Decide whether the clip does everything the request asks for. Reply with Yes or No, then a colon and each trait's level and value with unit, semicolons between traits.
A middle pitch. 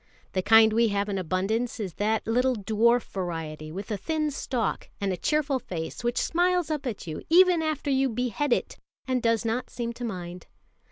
No: high, 230 Hz